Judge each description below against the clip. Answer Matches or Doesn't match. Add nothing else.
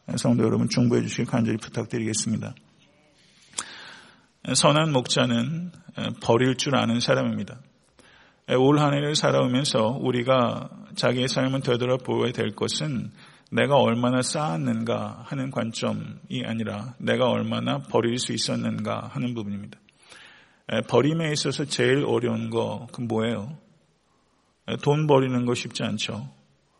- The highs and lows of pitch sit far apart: Doesn't match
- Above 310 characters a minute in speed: Doesn't match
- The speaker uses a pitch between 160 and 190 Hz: Doesn't match